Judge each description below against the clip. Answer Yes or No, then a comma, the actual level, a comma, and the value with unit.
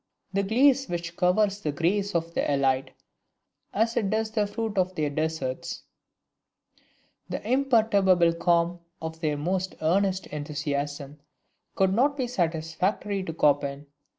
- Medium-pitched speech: Yes, medium, 175 Hz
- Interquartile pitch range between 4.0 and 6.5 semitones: Yes, average, 4.8 semitones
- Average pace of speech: No, slow, 130 wpm